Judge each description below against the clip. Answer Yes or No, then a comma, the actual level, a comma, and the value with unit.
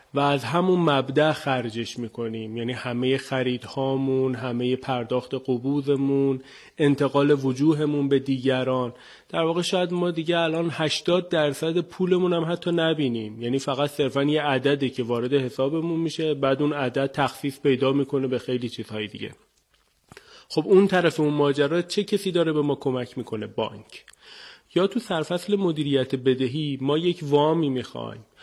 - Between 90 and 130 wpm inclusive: No, average, 145 wpm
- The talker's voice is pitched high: No, medium, 140 Hz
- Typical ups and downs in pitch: Yes, average, 3.7 semitones